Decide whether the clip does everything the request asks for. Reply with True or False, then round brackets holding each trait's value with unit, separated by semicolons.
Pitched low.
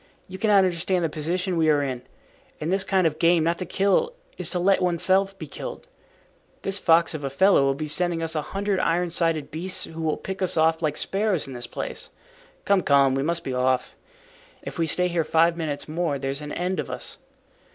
False (170 Hz)